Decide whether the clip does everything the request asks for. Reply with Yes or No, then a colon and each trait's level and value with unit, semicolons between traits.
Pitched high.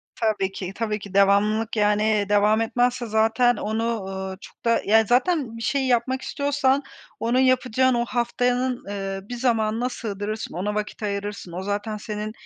Yes: high, 220 Hz